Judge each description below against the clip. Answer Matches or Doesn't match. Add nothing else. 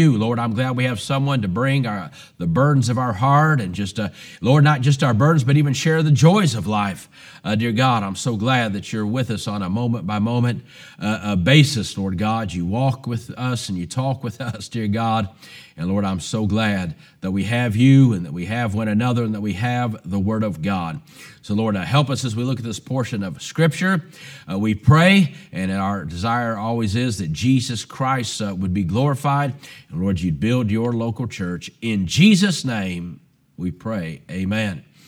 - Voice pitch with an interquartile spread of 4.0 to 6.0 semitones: Matches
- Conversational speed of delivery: Doesn't match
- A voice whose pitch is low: Matches